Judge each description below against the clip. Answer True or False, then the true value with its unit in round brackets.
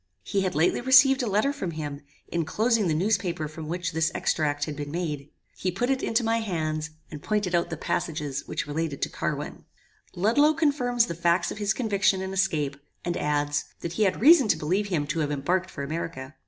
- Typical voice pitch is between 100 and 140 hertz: False (175 Hz)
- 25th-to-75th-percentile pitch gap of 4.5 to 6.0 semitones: True (5.6 semitones)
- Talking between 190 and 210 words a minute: True (205 wpm)